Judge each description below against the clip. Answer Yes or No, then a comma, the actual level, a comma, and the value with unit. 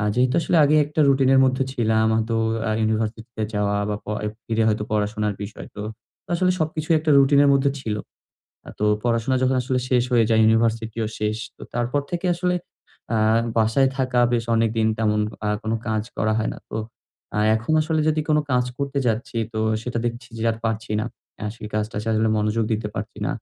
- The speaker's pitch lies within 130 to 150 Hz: No, low, 115 Hz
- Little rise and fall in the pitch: No, average, 3.5 semitones